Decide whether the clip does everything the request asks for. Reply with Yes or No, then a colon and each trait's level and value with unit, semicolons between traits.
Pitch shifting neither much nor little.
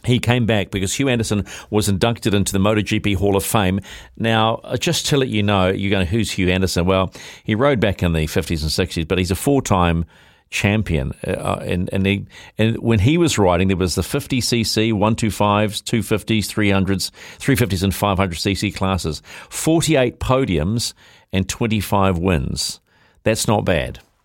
Yes: average, 3.1 semitones